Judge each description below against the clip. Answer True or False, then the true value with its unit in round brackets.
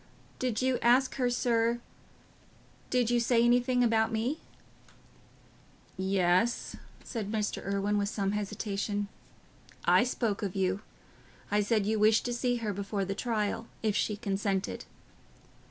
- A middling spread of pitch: True (3.1 semitones)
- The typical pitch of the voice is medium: False (220 Hz)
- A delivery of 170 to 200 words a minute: False (135 wpm)